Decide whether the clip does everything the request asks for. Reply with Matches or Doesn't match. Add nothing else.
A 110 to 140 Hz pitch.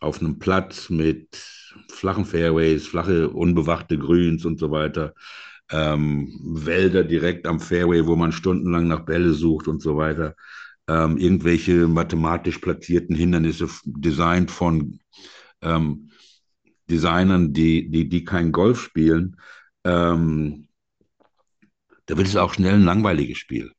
Doesn't match